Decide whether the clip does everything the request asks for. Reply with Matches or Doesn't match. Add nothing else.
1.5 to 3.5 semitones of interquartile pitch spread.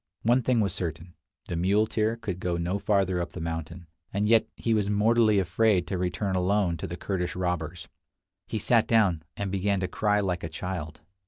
Matches